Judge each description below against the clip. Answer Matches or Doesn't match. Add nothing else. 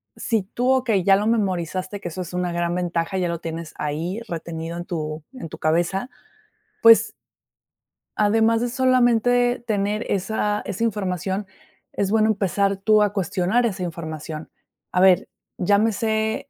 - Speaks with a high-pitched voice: Matches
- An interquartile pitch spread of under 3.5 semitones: Doesn't match